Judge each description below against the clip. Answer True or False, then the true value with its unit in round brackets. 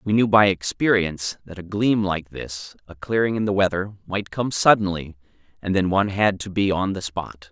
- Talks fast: True (210 wpm)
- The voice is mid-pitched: False (95 Hz)